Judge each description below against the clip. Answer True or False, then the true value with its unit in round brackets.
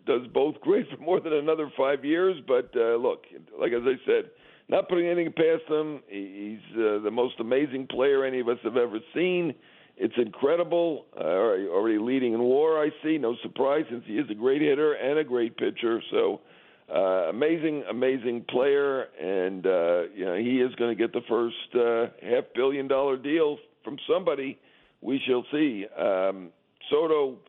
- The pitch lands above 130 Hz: True (140 Hz)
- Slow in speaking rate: False (185 wpm)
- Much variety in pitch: True (7.4 semitones)